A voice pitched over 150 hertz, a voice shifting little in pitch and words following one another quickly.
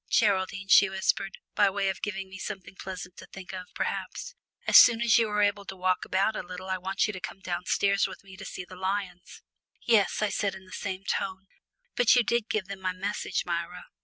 Yes: high, 190 Hz; narrow, 1.5 semitones; fast, 220 wpm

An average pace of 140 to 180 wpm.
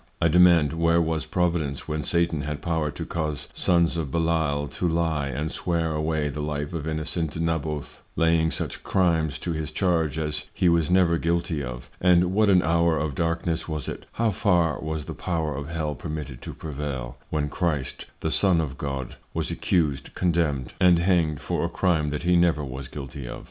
No: average, 190 wpm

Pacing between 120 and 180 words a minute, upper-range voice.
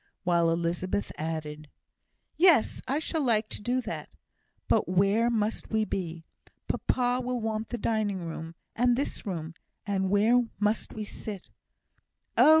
Yes: average, 145 wpm; high, 210 Hz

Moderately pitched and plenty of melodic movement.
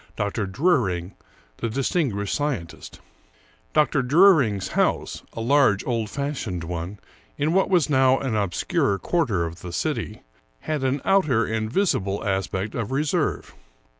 No: low, 115 Hz; wide, 6.7 semitones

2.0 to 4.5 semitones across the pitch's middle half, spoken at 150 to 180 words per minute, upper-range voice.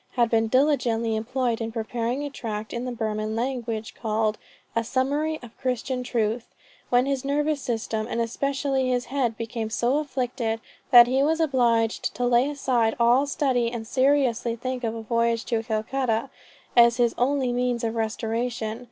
Yes: narrow, 2.4 semitones; average, 165 wpm; high, 240 Hz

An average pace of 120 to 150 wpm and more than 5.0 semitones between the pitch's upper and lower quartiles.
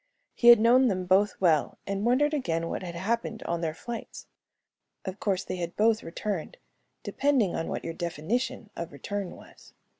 No: average, 175 wpm; wide, 5.4 semitones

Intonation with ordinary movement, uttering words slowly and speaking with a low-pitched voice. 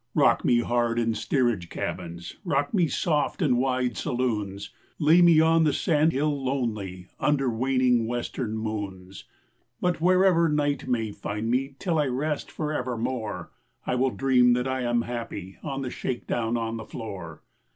No: average, 4.5 semitones; average, 155 wpm; low, 125 Hz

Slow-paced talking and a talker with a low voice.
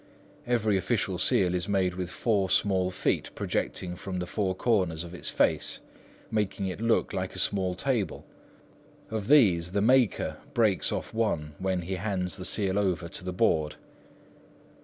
No: average, 160 wpm; very low, 95 Hz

